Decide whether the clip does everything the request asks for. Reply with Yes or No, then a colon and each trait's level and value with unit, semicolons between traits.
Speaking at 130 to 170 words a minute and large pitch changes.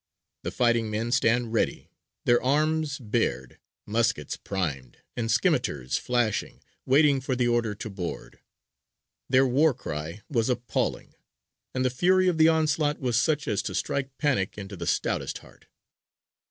No: average, 145 wpm; average, 4.6 semitones